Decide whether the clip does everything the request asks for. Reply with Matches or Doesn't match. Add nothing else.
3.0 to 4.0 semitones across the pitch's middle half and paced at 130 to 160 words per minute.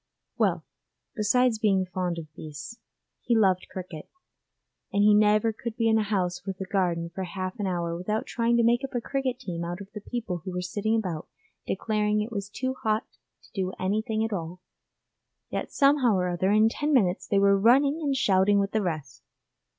Doesn't match